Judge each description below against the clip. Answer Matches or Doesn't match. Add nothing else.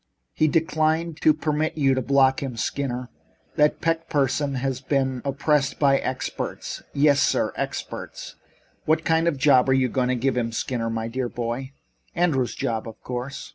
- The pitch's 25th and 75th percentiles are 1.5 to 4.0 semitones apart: Matches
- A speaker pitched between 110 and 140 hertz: Matches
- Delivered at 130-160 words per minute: Doesn't match